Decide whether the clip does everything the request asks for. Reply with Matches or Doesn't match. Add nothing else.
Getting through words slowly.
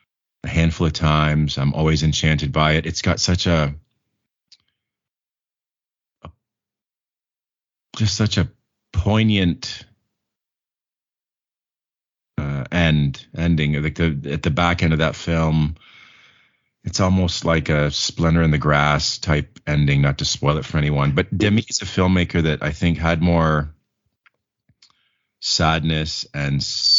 Matches